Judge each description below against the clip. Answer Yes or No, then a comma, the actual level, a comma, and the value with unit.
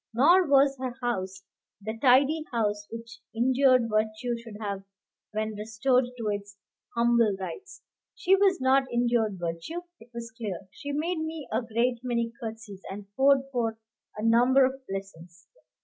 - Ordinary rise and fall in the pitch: Yes, average, 3.7 semitones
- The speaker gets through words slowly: No, average, 150 wpm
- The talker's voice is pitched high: Yes, high, 235 Hz